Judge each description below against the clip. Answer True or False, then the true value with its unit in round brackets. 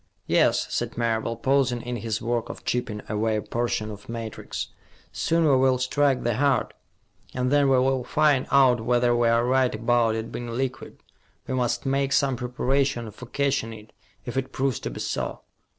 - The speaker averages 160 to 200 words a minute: True (180 wpm)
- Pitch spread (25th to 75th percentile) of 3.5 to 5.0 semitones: False (2.4 semitones)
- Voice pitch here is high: False (125 Hz)